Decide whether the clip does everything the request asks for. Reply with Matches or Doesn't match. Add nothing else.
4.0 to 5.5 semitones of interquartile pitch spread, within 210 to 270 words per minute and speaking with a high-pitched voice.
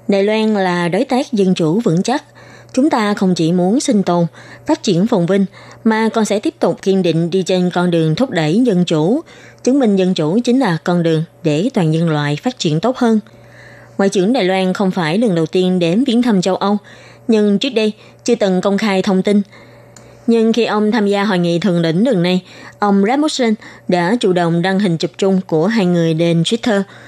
Matches